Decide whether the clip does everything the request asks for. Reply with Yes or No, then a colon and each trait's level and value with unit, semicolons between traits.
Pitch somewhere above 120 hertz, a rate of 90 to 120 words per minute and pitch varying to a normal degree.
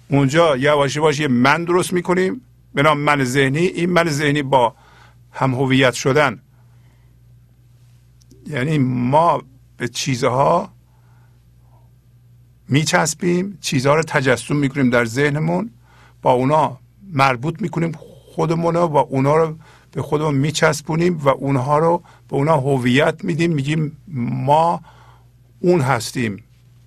Yes: medium, 140 Hz; average, 115 wpm; average, 4.3 semitones